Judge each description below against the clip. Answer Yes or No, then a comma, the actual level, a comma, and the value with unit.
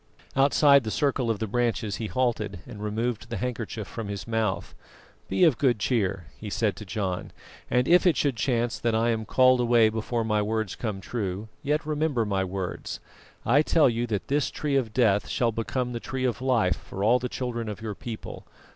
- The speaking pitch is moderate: No, low, 115 Hz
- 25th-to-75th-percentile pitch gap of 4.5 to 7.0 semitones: No, average, 3.1 semitones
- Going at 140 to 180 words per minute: No, average, 200 wpm